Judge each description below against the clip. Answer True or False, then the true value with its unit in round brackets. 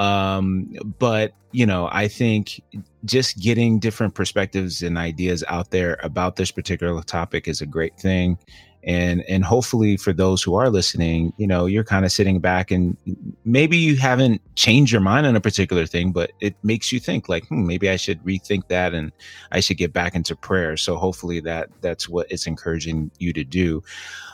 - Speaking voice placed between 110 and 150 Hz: False (95 Hz)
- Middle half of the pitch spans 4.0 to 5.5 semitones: False (3.2 semitones)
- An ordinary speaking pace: True (190 wpm)